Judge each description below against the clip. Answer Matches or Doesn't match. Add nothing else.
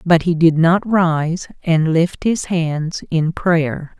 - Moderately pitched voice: Matches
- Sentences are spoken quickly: Doesn't match